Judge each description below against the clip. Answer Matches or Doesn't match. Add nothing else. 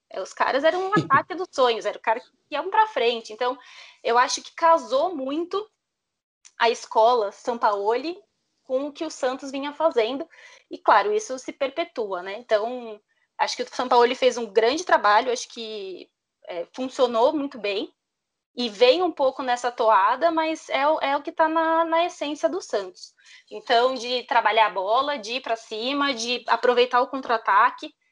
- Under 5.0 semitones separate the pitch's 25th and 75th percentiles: Doesn't match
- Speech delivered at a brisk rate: Doesn't match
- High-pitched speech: Matches